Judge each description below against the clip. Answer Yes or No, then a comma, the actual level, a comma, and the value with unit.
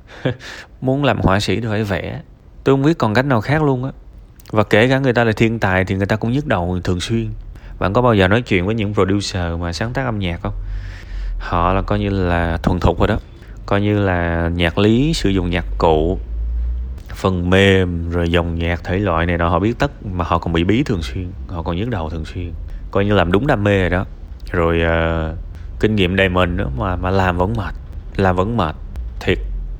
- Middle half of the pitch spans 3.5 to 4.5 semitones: Yes, average, 3.9 semitones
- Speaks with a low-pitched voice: Yes, very low, 95 Hz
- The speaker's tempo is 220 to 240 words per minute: Yes, average, 230 wpm